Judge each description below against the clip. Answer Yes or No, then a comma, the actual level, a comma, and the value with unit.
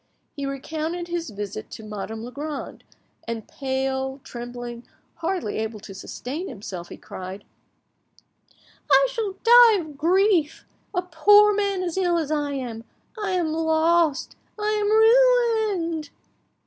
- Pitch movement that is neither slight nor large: No, wide, 7.5 semitones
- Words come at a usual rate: No, slow, 130 wpm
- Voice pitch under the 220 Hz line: No, very high, 315 Hz